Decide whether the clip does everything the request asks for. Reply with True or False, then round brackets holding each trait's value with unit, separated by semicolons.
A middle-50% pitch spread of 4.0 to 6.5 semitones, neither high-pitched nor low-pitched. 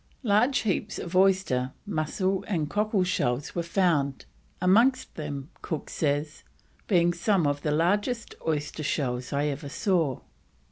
True (5.1 semitones; 170 Hz)